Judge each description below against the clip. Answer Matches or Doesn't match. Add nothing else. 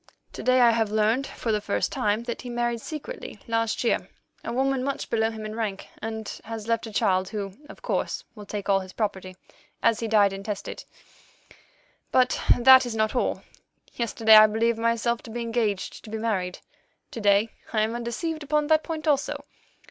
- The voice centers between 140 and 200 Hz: Doesn't match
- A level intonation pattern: Matches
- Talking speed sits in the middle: Matches